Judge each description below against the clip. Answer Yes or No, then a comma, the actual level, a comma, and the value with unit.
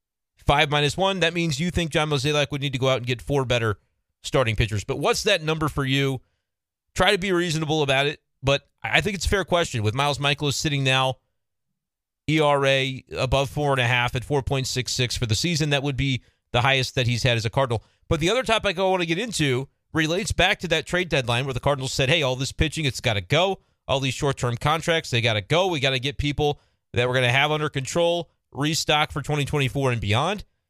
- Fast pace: Yes, fast, 235 wpm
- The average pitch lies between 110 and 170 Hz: Yes, medium, 140 Hz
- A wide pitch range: No, average, 3.7 semitones